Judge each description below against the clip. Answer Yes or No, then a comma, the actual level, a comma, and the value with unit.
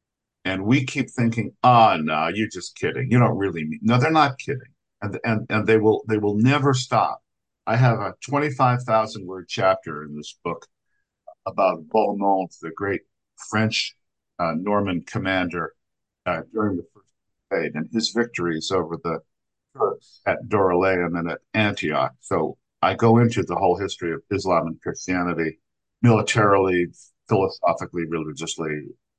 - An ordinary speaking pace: Yes, average, 155 wpm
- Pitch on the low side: Yes, low, 105 Hz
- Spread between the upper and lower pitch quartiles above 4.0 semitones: Yes, average, 4.9 semitones